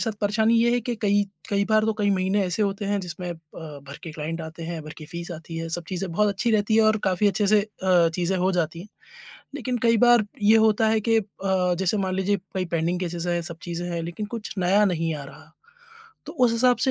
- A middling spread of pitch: Yes, average, 3.9 semitones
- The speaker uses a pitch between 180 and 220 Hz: Yes, high, 190 Hz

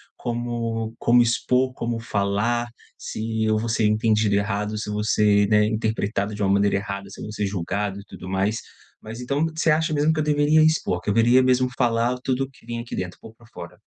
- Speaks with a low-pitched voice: Yes, low, 110 Hz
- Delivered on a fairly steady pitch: No, average, 3.0 semitones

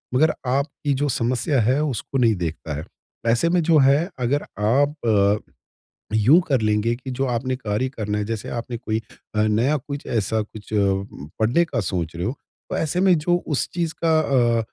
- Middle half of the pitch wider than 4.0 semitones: Yes, average, 5.1 semitones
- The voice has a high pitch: No, low, 125 Hz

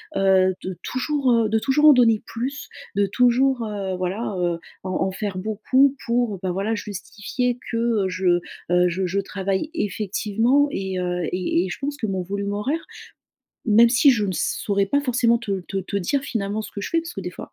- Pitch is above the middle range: Yes, high, 210 Hz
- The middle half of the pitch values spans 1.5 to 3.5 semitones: No, average, 4.4 semitones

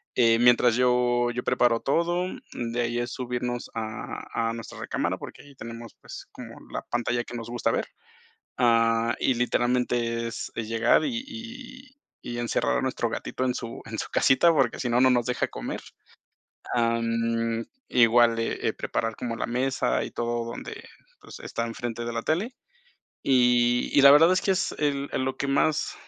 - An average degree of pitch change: No, narrow, 2.2 semitones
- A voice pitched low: Yes, low, 120 Hz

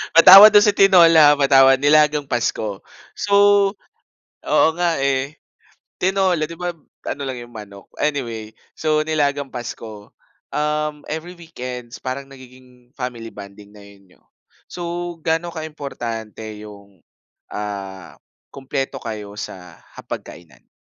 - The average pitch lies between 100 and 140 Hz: Yes, low, 135 Hz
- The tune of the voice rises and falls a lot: Yes, wide, 6.2 semitones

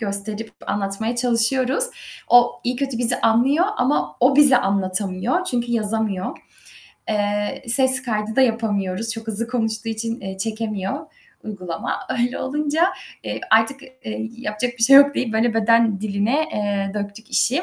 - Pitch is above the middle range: Yes, high, 225 Hz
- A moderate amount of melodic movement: Yes, average, 3.2 semitones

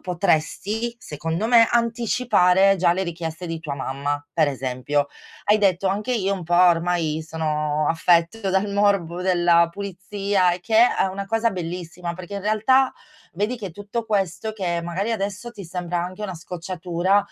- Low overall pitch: No, medium, 185 Hz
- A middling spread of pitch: Yes, average, 3.4 semitones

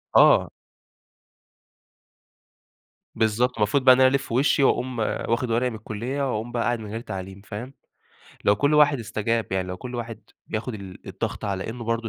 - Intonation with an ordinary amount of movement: Yes, average, 3.0 semitones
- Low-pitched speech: Yes, low, 115 Hz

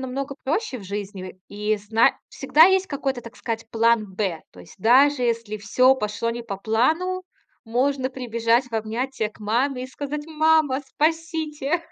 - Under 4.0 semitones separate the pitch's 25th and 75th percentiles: No, average, 4.6 semitones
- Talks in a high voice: Yes, very high, 250 Hz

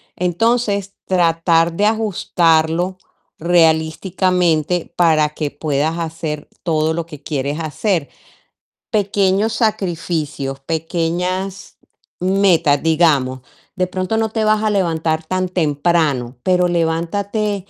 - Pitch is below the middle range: No, medium, 170 Hz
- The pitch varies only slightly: No, average, 3.1 semitones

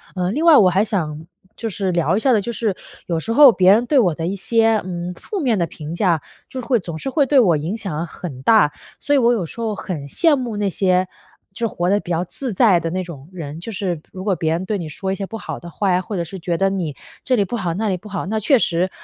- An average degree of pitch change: Yes, average, 4.6 semitones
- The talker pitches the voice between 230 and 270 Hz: No, high, 190 Hz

